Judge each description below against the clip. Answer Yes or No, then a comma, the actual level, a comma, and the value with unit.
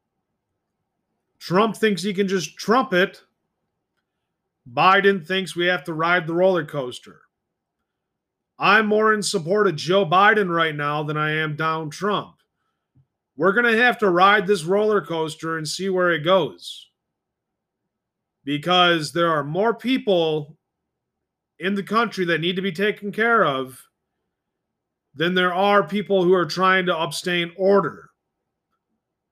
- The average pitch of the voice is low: No, medium, 185 Hz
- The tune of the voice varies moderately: Yes, average, 3.6 semitones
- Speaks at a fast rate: No, average, 140 wpm